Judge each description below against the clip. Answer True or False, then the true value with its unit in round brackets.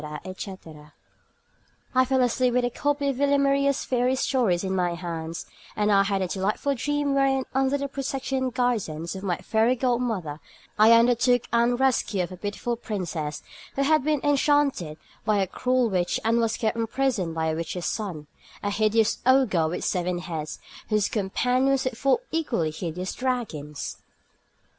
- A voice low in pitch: False (230 Hz)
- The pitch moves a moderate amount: False (6.4 semitones)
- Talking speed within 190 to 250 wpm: False (165 wpm)